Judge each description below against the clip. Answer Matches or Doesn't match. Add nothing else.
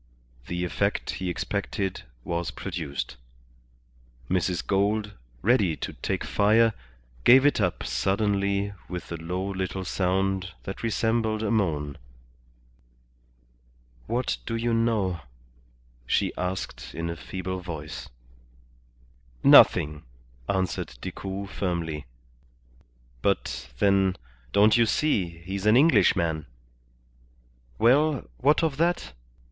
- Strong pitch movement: Doesn't match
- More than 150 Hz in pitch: Doesn't match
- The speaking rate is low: Matches